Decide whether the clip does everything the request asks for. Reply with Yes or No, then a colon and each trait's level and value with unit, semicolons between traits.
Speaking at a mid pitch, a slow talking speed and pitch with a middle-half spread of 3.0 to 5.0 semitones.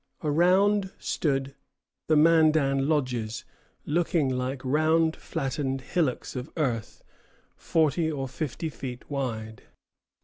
Yes: medium, 145 Hz; slow, 100 wpm; average, 3.5 semitones